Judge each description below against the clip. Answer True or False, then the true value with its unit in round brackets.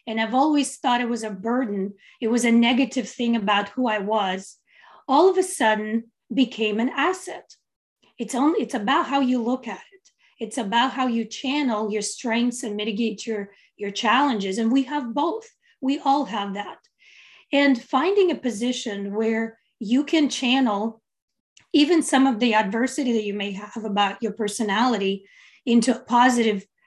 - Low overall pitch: False (240 Hz)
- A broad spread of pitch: False (3.9 semitones)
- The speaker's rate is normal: True (170 wpm)